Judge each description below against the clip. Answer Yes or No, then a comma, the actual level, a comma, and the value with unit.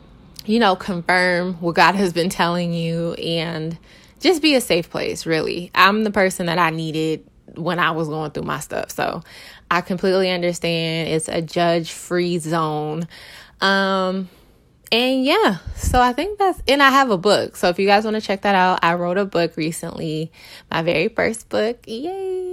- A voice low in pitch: No, medium, 180 Hz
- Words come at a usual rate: Yes, average, 180 wpm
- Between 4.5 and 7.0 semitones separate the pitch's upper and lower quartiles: No, average, 3.3 semitones